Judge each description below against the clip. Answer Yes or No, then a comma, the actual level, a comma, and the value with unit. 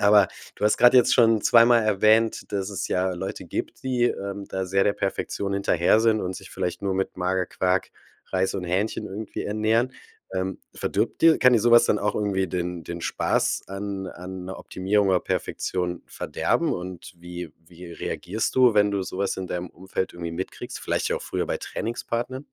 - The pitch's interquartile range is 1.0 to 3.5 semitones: Yes, average, 2.8 semitones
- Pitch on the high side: No, very low, 95 Hz